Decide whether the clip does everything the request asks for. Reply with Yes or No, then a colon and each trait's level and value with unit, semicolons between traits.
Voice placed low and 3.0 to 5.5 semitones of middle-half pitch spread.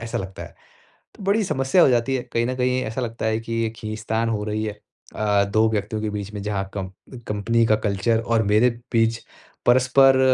No: low, 110 Hz; narrow, 2.6 semitones